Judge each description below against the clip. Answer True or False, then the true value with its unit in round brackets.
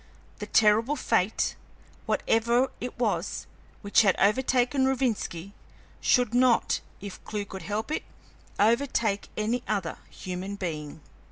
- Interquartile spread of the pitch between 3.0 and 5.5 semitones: True (3.8 semitones)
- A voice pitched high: True (215 Hz)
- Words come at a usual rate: False (115 wpm)